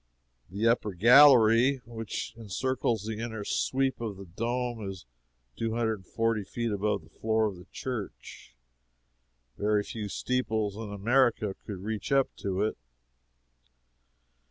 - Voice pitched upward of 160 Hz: No, low, 110 Hz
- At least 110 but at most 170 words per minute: Yes, slow, 135 wpm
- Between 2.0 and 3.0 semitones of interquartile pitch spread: Yes, narrow, 2.6 semitones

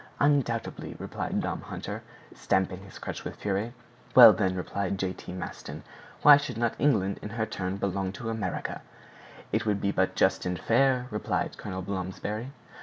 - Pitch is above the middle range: No, low, 100 Hz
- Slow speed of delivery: No, average, 170 wpm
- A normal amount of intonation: Yes, average, 3.5 semitones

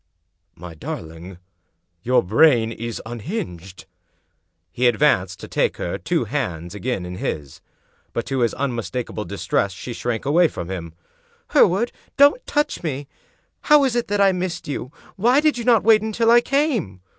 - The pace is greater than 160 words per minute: Yes, average, 170 wpm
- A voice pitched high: No, low, 125 Hz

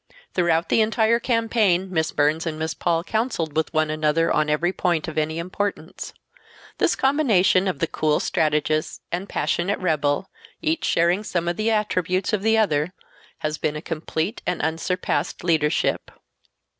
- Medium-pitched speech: Yes, medium, 170 Hz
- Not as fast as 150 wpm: No, average, 155 wpm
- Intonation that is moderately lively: Yes, average, 4.5 semitones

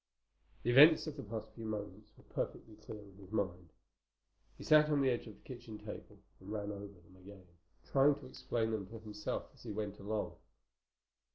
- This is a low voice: Yes, low, 110 Hz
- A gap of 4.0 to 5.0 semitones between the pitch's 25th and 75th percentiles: No, average, 3.1 semitones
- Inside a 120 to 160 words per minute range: No, average, 195 wpm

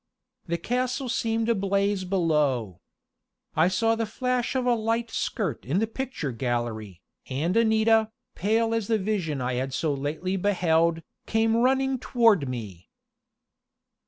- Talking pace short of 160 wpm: Yes, slow, 135 wpm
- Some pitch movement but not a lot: No, wide, 7.6 semitones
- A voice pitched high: Yes, high, 195 Hz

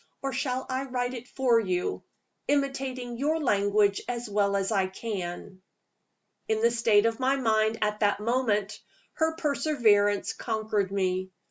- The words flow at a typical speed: Yes, average, 145 wpm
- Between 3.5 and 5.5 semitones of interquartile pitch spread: Yes, average, 4.2 semitones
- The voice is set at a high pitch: Yes, high, 225 Hz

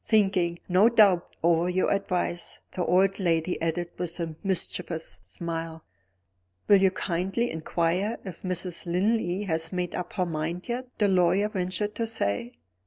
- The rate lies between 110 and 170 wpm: Yes, average, 150 wpm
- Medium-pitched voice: Yes, medium, 180 Hz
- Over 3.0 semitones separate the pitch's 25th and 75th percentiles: No, narrow, 2.6 semitones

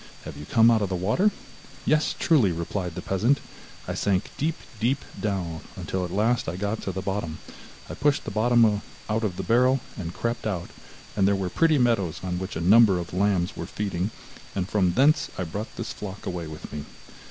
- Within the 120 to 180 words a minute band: No, fast, 205 wpm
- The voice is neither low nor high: No, low, 100 Hz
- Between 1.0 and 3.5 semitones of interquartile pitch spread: No, average, 4.4 semitones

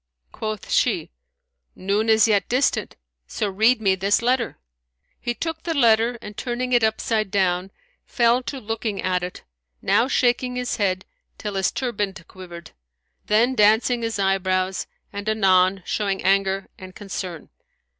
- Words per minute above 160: No, average, 145 wpm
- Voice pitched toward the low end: No, high, 210 Hz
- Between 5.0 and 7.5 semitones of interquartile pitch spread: No, average, 3.7 semitones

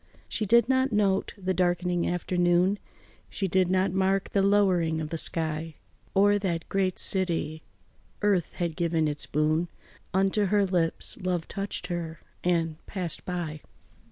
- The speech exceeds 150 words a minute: No, average, 145 wpm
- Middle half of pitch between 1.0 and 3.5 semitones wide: Yes, average, 2.8 semitones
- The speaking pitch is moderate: Yes, medium, 180 Hz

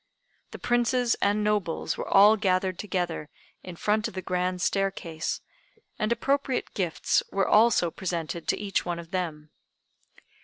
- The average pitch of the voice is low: No, high, 190 Hz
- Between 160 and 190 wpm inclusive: No, average, 145 wpm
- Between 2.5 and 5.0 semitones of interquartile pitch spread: Yes, average, 3.4 semitones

